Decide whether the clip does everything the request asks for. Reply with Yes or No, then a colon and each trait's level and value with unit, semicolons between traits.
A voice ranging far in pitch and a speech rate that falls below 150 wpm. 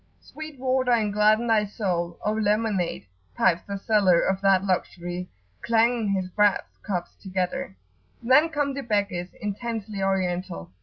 No: average, 3.7 semitones; average, 140 wpm